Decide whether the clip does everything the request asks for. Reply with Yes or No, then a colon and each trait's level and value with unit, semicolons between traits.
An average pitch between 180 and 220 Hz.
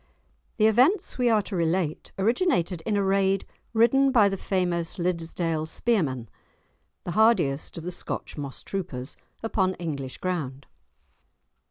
Yes: medium, 185 Hz